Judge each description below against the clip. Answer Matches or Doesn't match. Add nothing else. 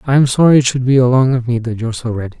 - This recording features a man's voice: Matches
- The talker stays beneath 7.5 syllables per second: Doesn't match